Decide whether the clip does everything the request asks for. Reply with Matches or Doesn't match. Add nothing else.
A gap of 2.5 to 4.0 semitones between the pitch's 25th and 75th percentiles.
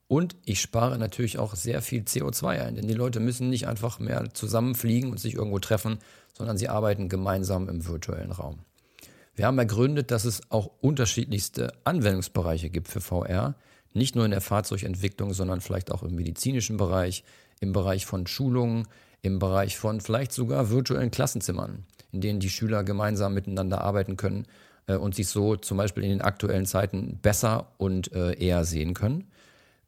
Matches